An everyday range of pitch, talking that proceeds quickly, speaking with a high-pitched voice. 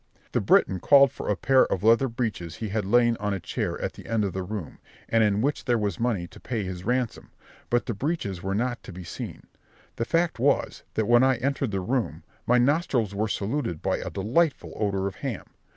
No: average, 4.4 semitones; fast, 220 wpm; low, 115 Hz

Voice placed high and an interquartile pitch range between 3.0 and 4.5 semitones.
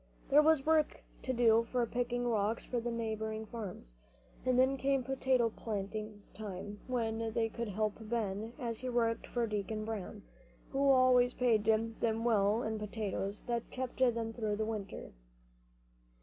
No: high, 225 Hz; narrow, 2.4 semitones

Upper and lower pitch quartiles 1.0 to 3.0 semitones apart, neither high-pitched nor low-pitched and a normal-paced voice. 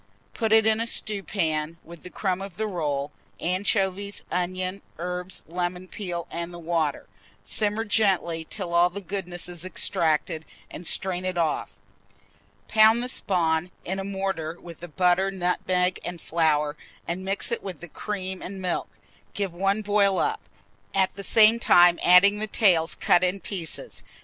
Yes: narrow, 2.5 semitones; medium, 180 Hz; average, 160 wpm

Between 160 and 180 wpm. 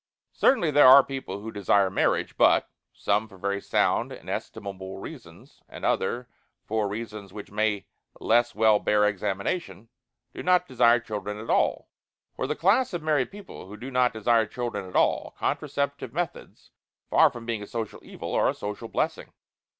Yes: average, 170 wpm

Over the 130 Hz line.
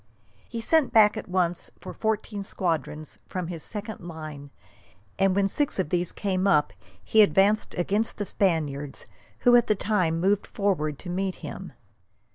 Yes: high, 190 Hz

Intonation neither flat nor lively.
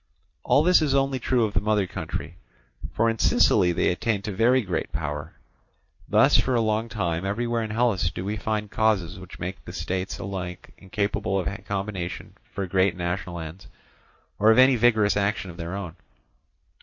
Yes: average, 3.6 semitones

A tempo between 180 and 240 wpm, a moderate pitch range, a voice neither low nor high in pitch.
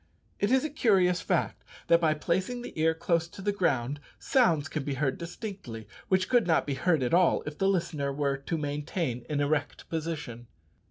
Yes: average, 195 wpm; average, 4.4 semitones; medium, 160 Hz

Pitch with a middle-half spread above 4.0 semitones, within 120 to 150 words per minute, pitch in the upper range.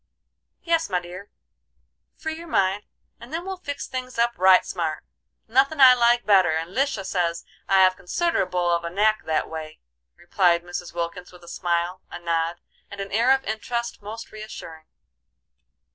No: wide, 5.6 semitones; average, 165 wpm; high, 195 Hz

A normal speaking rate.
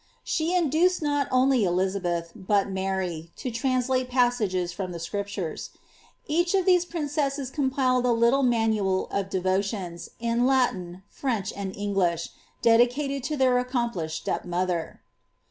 No: slow, 130 wpm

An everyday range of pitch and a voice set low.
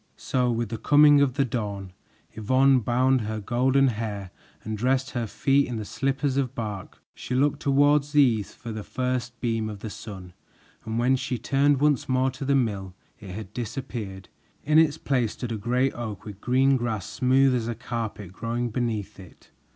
Yes: average, 3.6 semitones; low, 120 Hz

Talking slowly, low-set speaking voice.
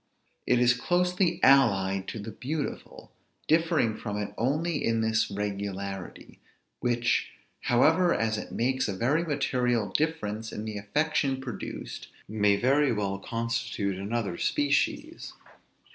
Yes: slow, 125 wpm; low, 115 Hz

